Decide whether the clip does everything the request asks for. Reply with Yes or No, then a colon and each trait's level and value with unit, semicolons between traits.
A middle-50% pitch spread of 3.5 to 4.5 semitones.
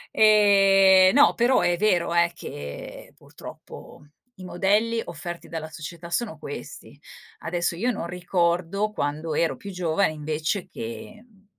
Yes: average, 3.8 semitones